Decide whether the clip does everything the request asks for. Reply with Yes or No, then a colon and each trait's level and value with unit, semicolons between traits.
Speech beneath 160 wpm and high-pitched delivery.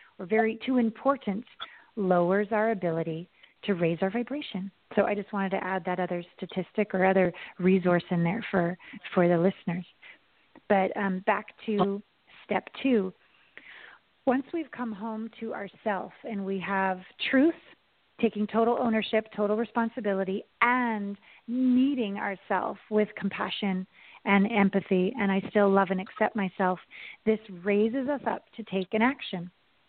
Yes: average, 145 wpm; high, 200 Hz